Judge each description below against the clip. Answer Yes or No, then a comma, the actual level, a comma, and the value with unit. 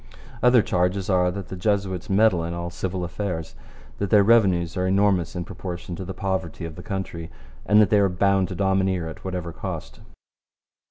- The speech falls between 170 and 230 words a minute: Yes, average, 185 wpm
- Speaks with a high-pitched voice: No, very low, 95 Hz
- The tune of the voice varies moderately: No, narrow, 2.1 semitones